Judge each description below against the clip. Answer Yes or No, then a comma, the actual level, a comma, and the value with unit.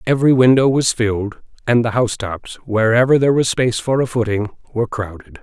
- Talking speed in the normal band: Yes, average, 190 wpm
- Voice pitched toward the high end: No, low, 120 Hz